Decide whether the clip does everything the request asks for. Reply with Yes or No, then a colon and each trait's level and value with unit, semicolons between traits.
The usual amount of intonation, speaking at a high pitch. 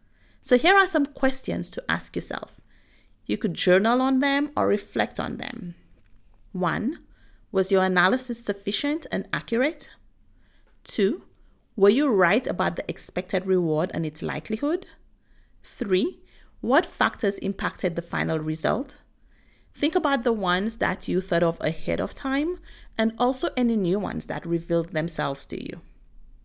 No: wide, 8.0 semitones; high, 195 Hz